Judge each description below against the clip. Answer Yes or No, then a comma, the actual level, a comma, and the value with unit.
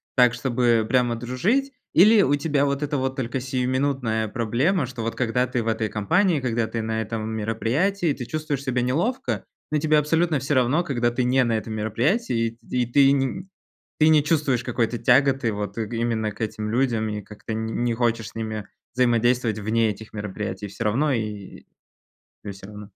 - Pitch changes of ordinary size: Yes, average, 3.9 semitones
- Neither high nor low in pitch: No, low, 120 Hz